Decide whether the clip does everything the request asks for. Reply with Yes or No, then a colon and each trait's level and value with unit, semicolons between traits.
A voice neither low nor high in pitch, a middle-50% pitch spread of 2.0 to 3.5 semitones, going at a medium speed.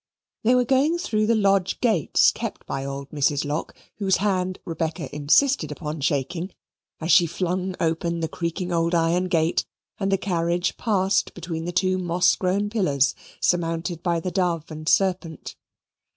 Yes: medium, 175 Hz; average, 2.8 semitones; average, 160 wpm